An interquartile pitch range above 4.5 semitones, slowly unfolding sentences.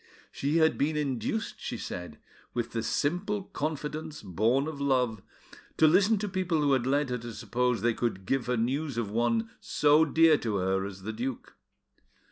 No: wide, 5.4 semitones; average, 180 wpm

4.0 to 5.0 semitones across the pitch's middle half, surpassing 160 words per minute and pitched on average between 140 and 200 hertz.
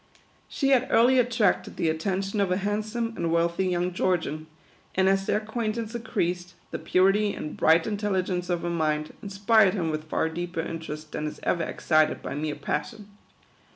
Yes: average, 4.4 semitones; average, 180 wpm; medium, 185 Hz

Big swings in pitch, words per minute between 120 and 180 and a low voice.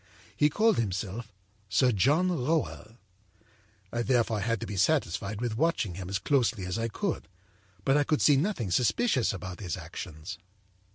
Yes: wide, 6.7 semitones; average, 160 wpm; low, 115 Hz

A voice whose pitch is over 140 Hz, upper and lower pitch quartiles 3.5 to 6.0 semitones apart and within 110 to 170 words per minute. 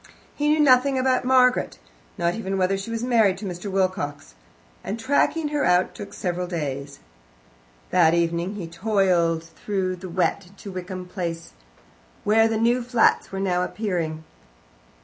Yes: high, 190 Hz; average, 4.4 semitones; average, 150 wpm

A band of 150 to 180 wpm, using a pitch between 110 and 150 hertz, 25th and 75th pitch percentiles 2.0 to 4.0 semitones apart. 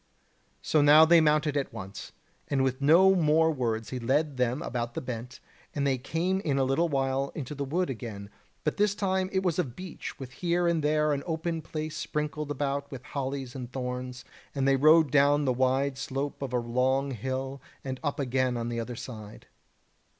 No: average, 195 wpm; medium, 140 Hz; average, 3.2 semitones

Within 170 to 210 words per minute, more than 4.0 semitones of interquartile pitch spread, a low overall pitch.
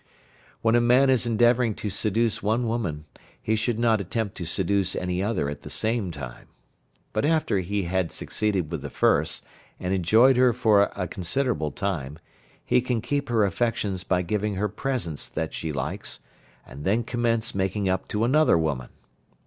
Yes: average, 175 wpm; average, 4.6 semitones; low, 105 Hz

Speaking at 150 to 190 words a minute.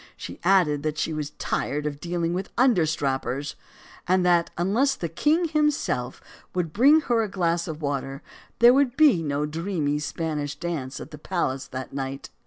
Yes: average, 170 wpm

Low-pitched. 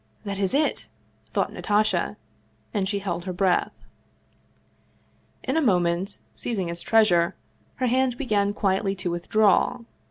No: high, 200 Hz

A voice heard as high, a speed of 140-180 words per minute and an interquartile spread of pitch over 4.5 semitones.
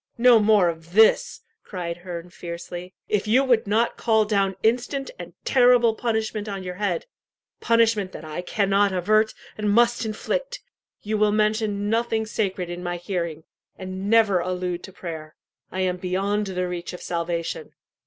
No: high, 200 Hz; average, 160 wpm; average, 3.6 semitones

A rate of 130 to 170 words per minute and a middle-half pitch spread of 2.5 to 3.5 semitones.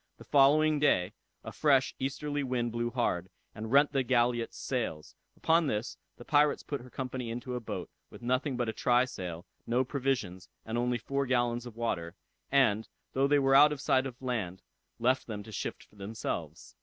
No: average, 190 wpm; average, 3.1 semitones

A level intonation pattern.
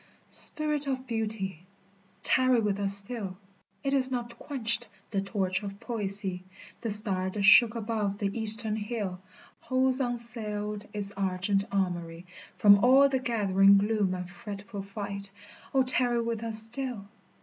No: average, 3.2 semitones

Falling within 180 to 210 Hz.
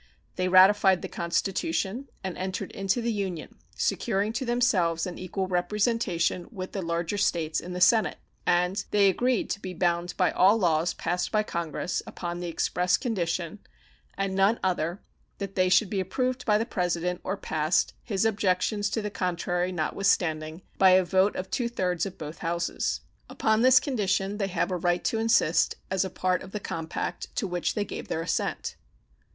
Yes: medium, 185 Hz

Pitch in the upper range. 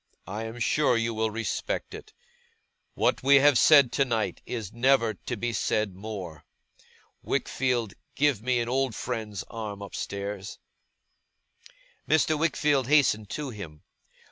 No: low, 115 Hz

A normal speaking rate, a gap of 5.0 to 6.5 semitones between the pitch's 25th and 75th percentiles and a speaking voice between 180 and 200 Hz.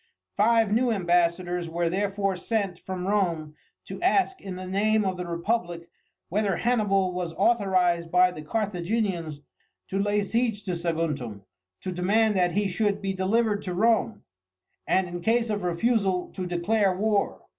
No: average, 155 wpm; average, 3.3 semitones; high, 190 Hz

